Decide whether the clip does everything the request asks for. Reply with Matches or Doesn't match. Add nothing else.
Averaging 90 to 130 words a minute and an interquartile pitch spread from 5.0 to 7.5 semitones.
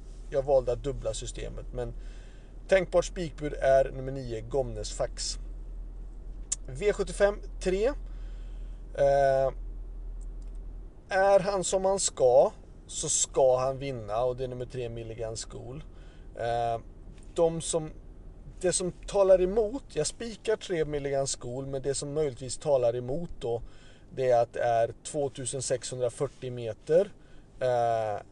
Matches